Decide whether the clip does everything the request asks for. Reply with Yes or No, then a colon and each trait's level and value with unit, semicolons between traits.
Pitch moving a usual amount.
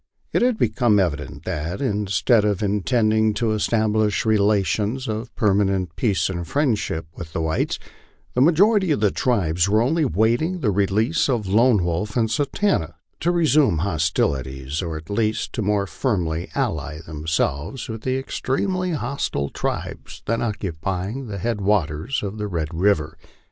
No: wide, 5.8 semitones